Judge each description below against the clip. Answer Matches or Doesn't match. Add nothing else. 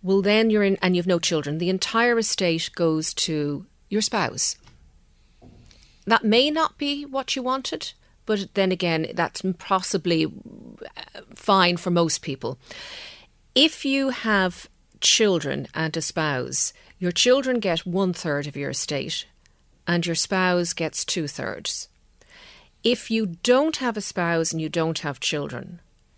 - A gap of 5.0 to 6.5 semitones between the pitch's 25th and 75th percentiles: Matches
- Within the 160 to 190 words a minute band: Doesn't match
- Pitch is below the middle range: Doesn't match